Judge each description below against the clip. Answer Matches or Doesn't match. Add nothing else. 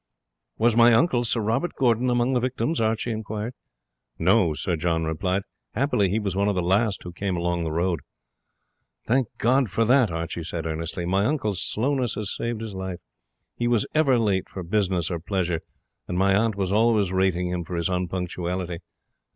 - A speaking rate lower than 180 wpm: Doesn't match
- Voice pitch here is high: Doesn't match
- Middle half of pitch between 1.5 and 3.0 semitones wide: Doesn't match